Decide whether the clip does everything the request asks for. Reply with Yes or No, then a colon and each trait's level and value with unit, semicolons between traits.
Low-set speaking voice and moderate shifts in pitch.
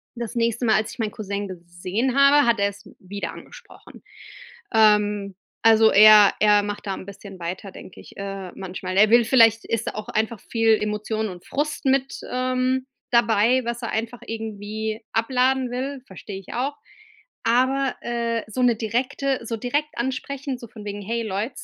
No: high, 225 Hz; average, 3.4 semitones